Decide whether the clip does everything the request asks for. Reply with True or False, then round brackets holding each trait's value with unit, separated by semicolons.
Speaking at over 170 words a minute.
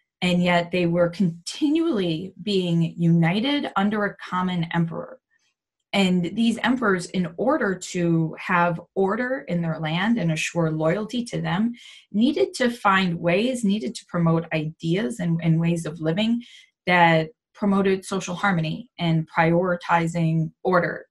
False (135 wpm)